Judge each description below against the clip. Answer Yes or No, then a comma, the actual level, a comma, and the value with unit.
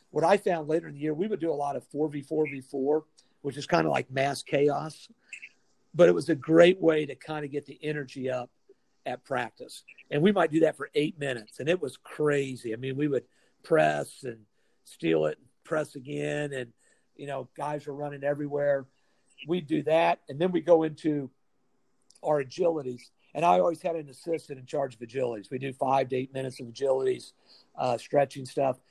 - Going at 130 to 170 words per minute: No, average, 200 wpm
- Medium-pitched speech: Yes, medium, 145 Hz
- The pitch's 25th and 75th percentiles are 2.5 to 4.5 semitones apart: Yes, average, 3.0 semitones